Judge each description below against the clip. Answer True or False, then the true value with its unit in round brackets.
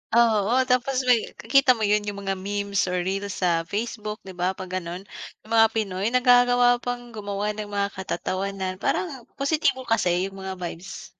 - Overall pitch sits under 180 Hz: False (205 Hz)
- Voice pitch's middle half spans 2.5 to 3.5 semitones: False (3.9 semitones)